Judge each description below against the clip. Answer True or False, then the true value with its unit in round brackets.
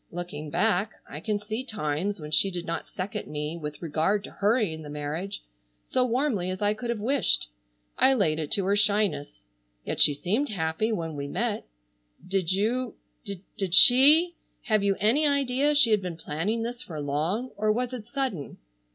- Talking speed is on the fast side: False (175 wpm)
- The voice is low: False (200 Hz)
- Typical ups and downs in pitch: False (6.1 semitones)